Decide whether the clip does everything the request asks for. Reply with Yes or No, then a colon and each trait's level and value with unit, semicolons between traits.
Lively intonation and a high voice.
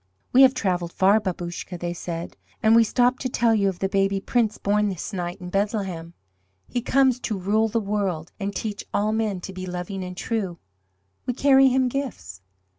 No: average, 4.0 semitones; high, 200 Hz